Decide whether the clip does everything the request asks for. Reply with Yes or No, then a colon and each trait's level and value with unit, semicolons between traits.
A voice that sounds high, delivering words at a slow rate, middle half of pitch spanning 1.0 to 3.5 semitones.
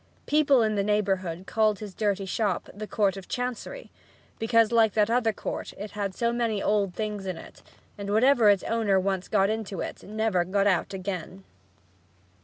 No: high, 210 Hz; average, 180 wpm; narrow, 2.4 semitones